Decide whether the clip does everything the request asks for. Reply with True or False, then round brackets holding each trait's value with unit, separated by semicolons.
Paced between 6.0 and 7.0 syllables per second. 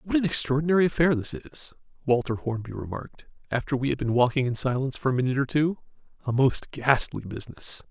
True (6.3 syllables/s)